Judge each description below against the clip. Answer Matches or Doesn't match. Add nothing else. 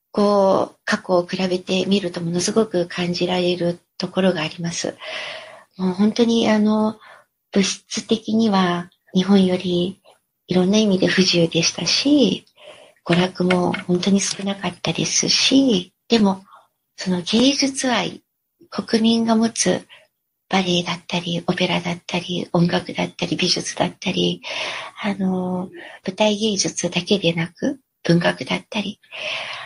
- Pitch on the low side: Doesn't match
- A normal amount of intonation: Matches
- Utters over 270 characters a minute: Doesn't match